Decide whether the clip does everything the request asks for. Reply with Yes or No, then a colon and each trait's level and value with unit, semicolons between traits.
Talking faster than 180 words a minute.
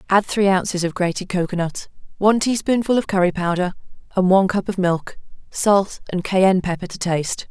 No: average, 175 wpm